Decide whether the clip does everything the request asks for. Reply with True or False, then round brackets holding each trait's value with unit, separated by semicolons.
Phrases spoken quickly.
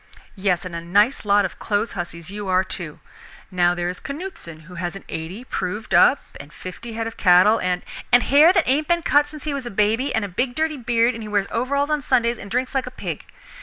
True (245 wpm)